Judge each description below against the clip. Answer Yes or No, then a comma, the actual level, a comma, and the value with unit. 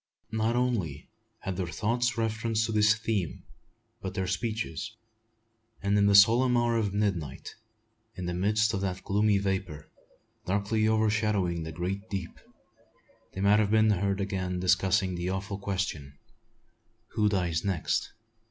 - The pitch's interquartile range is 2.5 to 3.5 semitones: Yes, average, 2.9 semitones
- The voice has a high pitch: No, low, 100 Hz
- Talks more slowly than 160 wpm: Yes, average, 145 wpm